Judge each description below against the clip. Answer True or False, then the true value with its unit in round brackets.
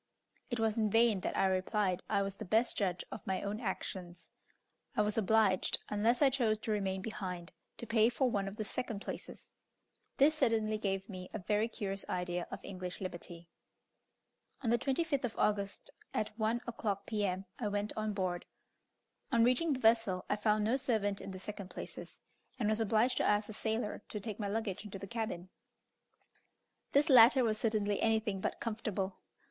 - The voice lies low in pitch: False (210 Hz)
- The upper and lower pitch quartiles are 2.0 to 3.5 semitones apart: True (2.7 semitones)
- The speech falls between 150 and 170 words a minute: False (185 wpm)